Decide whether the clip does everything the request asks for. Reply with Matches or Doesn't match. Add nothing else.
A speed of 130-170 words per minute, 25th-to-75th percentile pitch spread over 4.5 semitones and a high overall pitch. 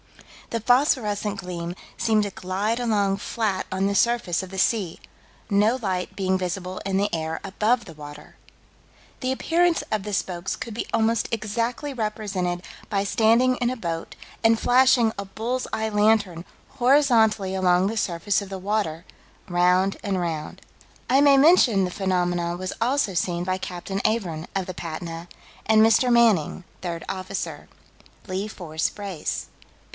Doesn't match